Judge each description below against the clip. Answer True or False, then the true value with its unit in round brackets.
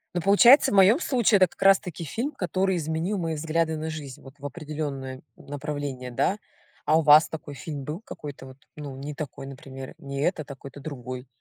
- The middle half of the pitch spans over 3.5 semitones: True (4.2 semitones)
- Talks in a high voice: False (150 Hz)